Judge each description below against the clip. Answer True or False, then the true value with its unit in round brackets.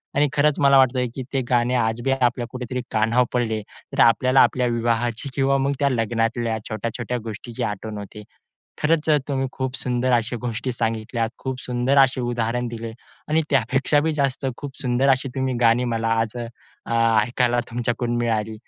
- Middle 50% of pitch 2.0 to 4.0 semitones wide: True (2.4 semitones)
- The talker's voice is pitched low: True (120 Hz)